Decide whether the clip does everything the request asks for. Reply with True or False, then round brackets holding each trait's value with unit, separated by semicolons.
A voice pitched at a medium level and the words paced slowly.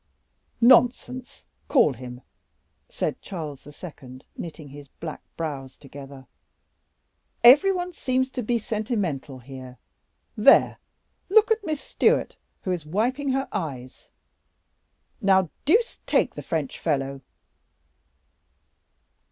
True (170 Hz; 105 wpm)